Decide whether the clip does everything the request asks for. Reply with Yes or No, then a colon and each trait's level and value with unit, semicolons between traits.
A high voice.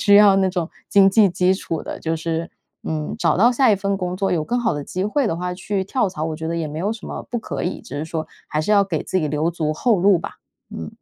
No: medium, 180 Hz